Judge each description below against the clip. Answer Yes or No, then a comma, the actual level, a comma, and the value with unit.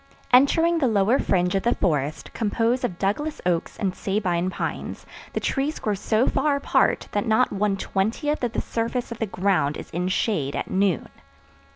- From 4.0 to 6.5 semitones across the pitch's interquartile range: Yes, average, 4.9 semitones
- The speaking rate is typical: Yes, average, 180 wpm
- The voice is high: Yes, high, 205 Hz